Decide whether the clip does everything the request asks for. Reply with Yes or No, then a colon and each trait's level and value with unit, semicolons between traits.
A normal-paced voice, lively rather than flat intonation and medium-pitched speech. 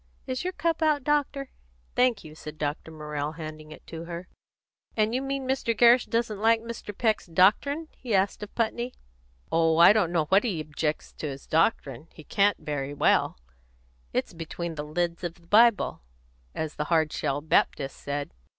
Yes: average, 180 wpm; wide, 7.1 semitones; medium, 175 Hz